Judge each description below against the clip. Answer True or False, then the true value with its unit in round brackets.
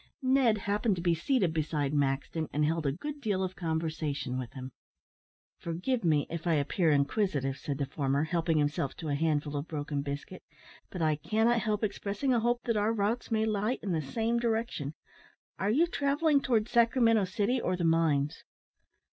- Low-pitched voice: False (175 Hz)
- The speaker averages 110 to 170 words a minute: False (180 wpm)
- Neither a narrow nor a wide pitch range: False (7.1 semitones)